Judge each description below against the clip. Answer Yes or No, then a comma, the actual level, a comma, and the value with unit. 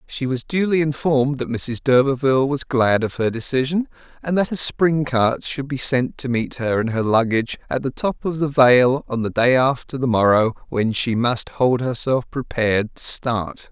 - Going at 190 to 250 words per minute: Yes, average, 200 wpm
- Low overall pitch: Yes, low, 130 Hz